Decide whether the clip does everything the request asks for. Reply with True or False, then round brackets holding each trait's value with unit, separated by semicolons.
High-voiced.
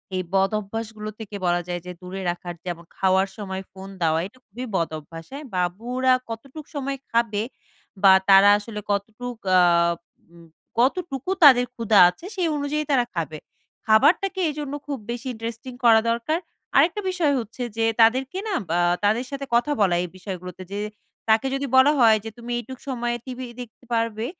True (225 Hz)